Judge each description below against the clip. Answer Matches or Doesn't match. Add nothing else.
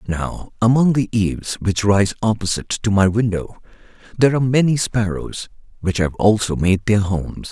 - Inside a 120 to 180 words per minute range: Matches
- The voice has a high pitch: Doesn't match